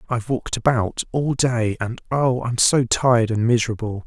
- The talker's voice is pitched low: Yes, low, 120 Hz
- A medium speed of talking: Yes, average, 150 wpm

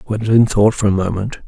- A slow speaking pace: No, fast, 205 wpm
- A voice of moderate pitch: No, low, 105 Hz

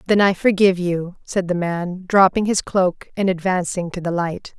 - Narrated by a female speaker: Yes, female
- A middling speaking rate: Yes, average, 195 wpm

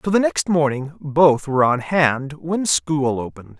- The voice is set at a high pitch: No, medium, 150 Hz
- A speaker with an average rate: Yes, average, 185 wpm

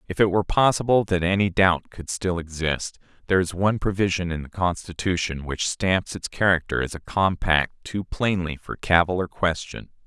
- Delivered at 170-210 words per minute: Yes, average, 180 wpm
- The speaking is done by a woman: No, male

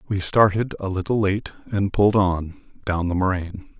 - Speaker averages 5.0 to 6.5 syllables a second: Yes, 5.4 syllables/s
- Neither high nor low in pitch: No, very low, 95 Hz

